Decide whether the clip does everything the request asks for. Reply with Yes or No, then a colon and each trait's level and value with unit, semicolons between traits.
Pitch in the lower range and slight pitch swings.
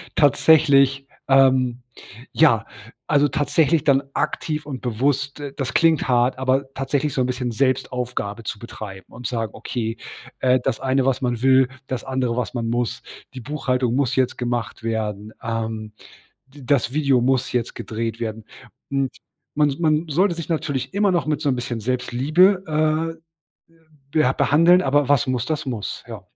No: low, 130 Hz; average, 3.3 semitones